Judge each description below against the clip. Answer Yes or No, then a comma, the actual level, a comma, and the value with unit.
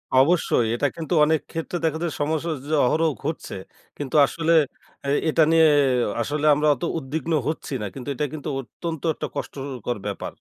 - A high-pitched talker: No, medium, 155 Hz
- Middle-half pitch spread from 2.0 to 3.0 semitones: Yes, narrow, 2.6 semitones